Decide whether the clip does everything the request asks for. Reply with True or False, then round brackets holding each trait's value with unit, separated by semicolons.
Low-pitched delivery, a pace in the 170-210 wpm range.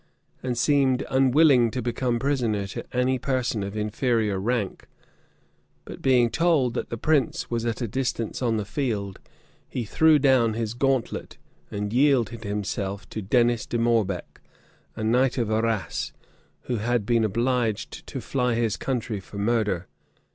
False (120 Hz; 150 wpm)